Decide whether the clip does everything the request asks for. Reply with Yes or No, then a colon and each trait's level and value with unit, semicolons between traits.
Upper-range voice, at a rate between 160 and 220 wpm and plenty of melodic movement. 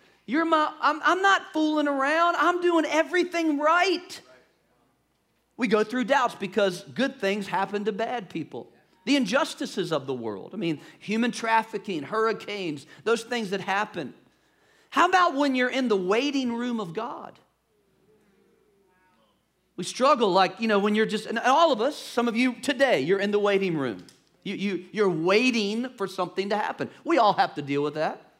Yes: high, 225 Hz; average, 175 wpm; wide, 6.5 semitones